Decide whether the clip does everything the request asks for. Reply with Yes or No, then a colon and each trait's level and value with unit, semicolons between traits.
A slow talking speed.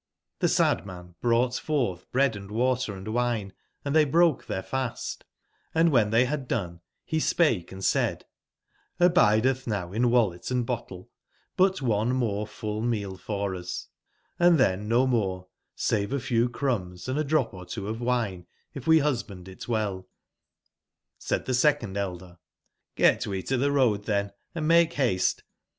No: average, 155 wpm